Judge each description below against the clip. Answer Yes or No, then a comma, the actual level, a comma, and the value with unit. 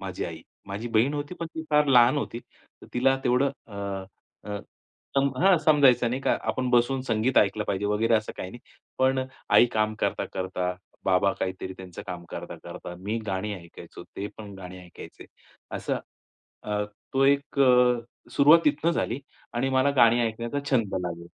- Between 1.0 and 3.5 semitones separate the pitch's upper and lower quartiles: No, average, 5.1 semitones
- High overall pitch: No, low, 115 Hz